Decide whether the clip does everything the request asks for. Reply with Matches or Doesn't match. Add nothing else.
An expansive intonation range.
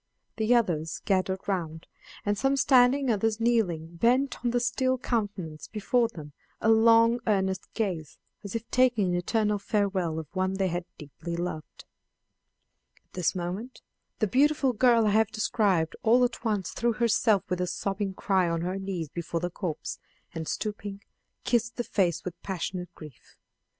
Doesn't match